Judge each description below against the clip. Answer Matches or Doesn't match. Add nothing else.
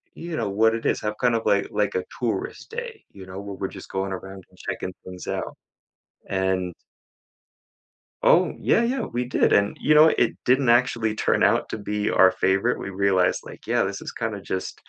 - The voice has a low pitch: Matches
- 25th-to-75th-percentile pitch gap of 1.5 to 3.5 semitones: Doesn't match